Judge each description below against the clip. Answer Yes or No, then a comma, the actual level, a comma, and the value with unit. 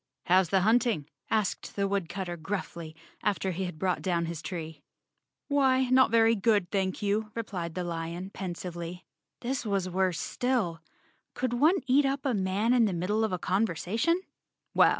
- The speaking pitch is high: Yes, high, 195 Hz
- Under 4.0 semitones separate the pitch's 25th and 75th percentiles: No, average, 4.6 semitones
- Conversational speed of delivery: Yes, average, 160 wpm